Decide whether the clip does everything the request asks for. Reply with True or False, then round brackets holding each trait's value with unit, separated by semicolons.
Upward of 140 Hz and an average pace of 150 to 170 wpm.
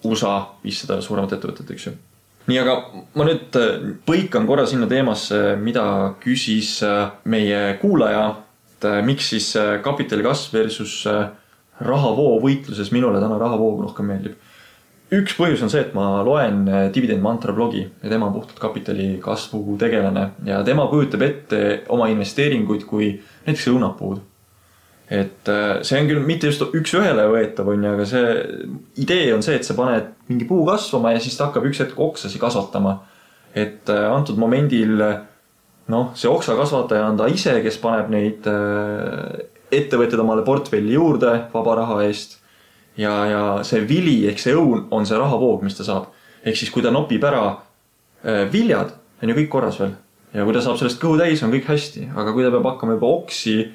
False (110 Hz; 165 wpm)